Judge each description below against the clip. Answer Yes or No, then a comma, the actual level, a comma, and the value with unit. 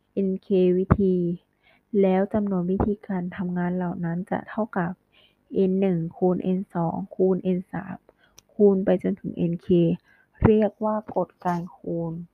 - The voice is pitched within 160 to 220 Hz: Yes, medium, 185 Hz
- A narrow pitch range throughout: Yes, narrow, 1.6 semitones